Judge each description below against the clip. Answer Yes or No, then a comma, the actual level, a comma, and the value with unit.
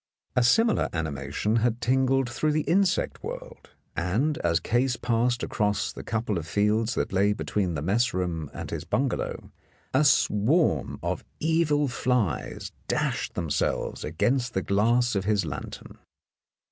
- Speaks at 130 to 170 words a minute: Yes, average, 145 wpm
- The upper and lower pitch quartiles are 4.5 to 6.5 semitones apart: Yes, average, 5.3 semitones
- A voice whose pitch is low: Yes, low, 115 Hz